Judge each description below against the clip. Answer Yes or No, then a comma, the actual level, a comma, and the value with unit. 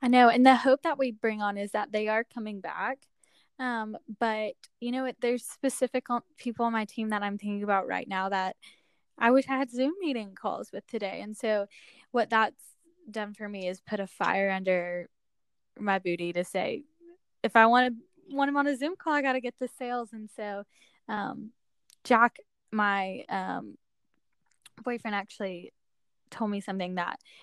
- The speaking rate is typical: Yes, average, 190 wpm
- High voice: Yes, high, 225 Hz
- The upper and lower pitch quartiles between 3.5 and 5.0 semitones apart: Yes, average, 3.9 semitones